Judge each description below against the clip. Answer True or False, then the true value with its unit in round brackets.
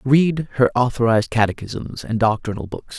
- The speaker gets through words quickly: False (140 wpm)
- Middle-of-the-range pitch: False (120 Hz)